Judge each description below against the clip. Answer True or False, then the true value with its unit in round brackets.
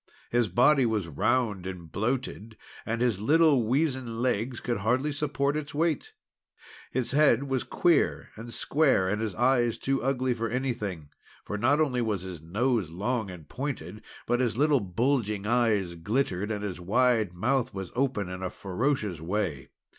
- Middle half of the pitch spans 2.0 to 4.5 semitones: False (5.0 semitones)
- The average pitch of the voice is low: True (115 Hz)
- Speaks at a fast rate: False (160 wpm)